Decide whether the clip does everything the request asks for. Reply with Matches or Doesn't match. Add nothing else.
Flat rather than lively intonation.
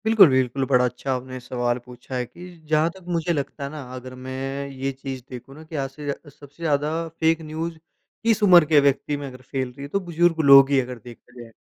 Doesn't match